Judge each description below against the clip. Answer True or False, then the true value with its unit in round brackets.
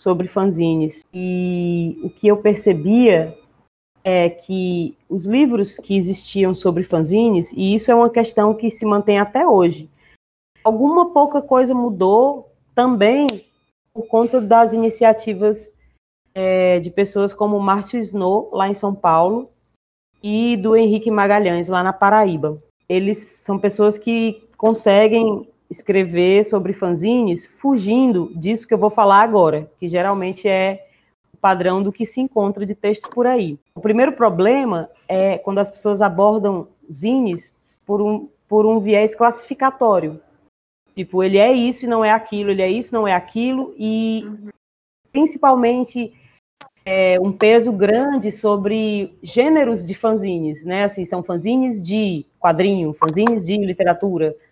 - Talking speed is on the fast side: False (140 wpm)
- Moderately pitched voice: False (205 Hz)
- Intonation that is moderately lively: True (3.4 semitones)